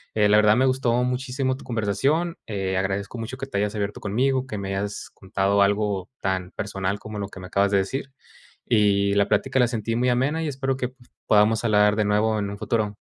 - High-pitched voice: No, low, 105 Hz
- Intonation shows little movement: No, average, 3.9 semitones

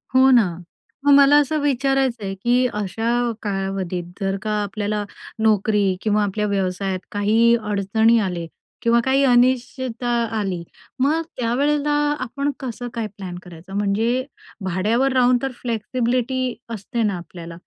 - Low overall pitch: No, high, 225 Hz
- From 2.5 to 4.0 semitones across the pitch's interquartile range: No, average, 4.5 semitones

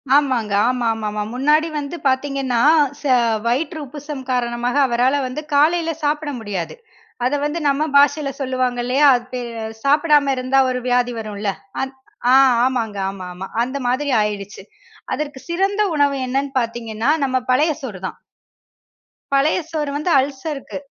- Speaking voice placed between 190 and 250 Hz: No, very high, 265 Hz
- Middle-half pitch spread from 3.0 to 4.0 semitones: Yes, average, 3.4 semitones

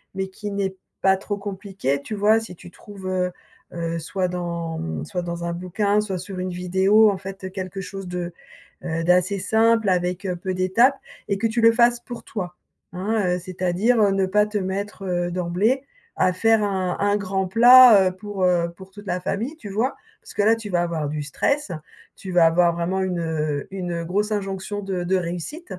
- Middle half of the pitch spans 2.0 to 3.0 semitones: Yes, narrow, 2.6 semitones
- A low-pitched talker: No, high, 190 Hz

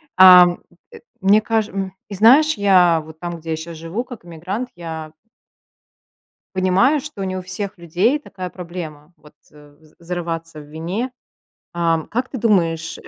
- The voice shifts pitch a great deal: No, average, 3.8 semitones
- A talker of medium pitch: Yes, medium, 180 Hz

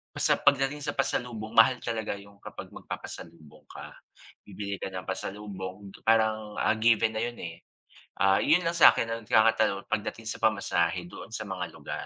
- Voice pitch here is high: No, low, 110 Hz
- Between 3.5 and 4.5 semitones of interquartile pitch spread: No, average, 2.8 semitones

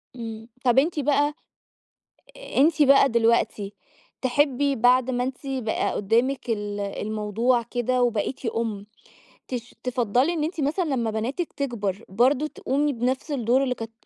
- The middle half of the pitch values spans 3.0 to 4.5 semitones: Yes, average, 3.5 semitones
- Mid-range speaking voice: No, high, 245 Hz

